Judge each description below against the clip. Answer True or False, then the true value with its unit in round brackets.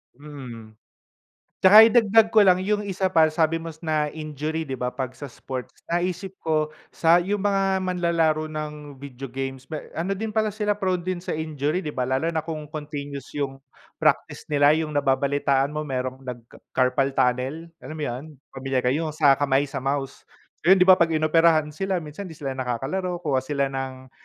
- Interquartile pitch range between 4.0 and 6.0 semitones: True (4.3 semitones)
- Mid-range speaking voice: True (150 Hz)